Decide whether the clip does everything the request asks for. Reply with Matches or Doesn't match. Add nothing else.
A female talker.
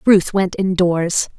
Matches